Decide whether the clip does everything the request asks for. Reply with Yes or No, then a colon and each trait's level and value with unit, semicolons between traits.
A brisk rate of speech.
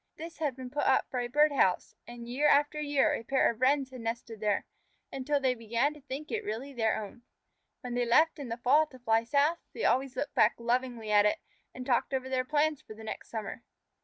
Yes: fast, 235 wpm